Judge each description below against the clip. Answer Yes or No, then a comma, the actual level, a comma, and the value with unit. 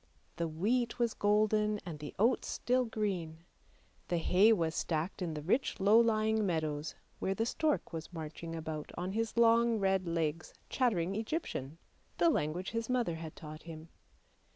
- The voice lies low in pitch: No, high, 190 Hz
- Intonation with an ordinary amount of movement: No, wide, 5.8 semitones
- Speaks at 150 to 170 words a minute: Yes, average, 160 wpm